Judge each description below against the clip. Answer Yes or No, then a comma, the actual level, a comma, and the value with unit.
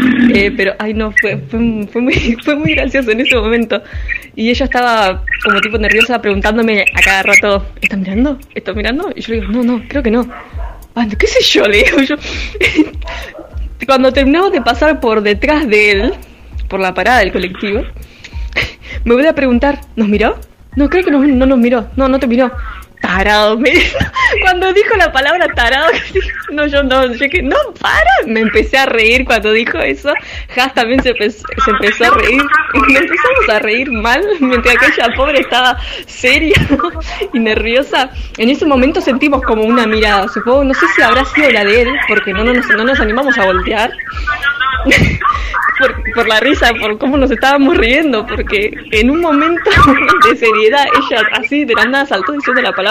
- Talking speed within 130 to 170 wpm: No, average, 185 wpm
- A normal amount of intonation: Yes, average, 4.3 semitones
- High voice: Yes, very high, 255 Hz